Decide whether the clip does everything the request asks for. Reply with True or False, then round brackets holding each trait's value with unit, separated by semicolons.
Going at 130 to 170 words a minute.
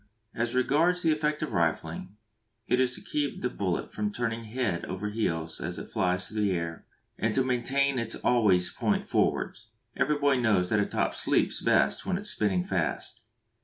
False (190 wpm)